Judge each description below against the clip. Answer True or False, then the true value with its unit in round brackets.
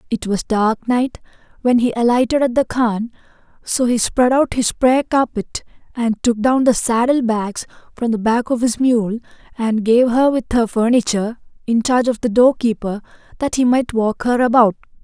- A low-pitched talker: False (235 Hz)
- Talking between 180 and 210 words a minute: True (190 wpm)